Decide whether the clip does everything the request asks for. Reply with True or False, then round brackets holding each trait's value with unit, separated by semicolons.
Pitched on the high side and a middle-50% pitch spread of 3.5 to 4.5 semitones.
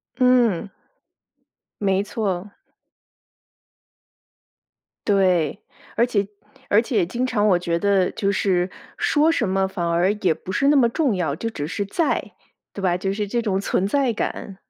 True (200 Hz; 4.0 semitones)